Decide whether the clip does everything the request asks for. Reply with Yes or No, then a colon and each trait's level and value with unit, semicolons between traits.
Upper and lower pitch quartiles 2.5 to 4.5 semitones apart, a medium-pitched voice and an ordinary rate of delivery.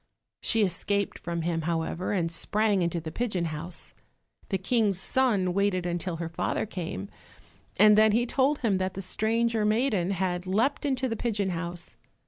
No: average, 4.1 semitones; high, 195 Hz; average, 165 wpm